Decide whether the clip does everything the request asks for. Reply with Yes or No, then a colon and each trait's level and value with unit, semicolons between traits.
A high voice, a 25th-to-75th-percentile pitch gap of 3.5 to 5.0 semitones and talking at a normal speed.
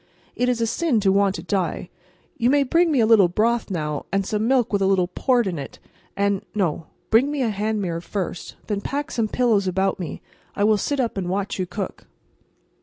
No: high, 205 Hz; average, 3.8 semitones; fast, 225 wpm